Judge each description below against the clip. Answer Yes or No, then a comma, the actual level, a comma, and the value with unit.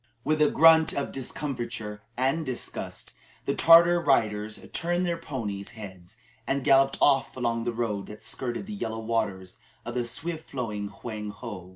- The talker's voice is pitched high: No, low, 120 Hz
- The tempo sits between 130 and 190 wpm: Yes, average, 160 wpm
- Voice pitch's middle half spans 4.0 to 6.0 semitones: Yes, wide, 5.6 semitones